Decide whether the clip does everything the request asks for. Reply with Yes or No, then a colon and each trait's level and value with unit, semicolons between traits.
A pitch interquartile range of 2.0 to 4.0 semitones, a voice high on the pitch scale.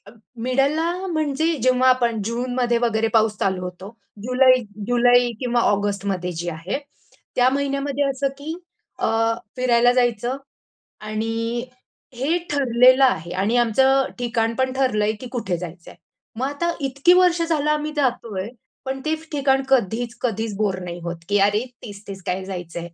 No: average, 4.4 semitones; high, 245 Hz